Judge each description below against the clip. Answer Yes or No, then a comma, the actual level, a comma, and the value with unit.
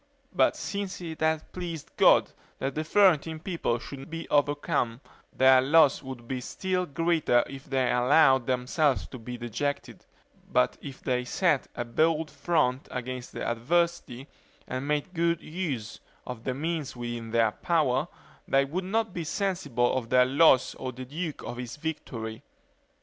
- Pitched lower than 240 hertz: Yes, medium, 140 Hz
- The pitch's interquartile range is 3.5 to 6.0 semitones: Yes, average, 4.7 semitones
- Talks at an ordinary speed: Yes, average, 155 wpm